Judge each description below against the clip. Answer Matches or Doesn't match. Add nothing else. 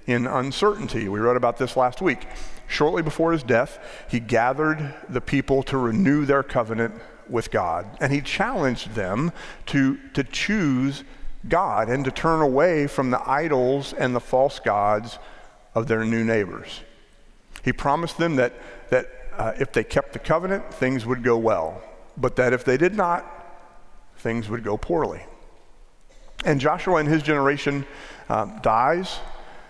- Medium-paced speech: Matches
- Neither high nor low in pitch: Doesn't match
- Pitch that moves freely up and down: Doesn't match